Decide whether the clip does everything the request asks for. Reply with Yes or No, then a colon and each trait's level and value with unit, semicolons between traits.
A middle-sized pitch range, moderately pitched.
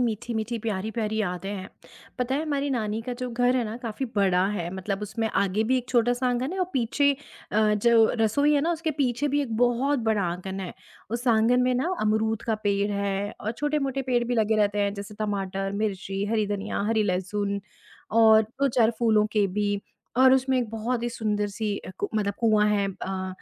No: average, 3.3 semitones; high, 220 Hz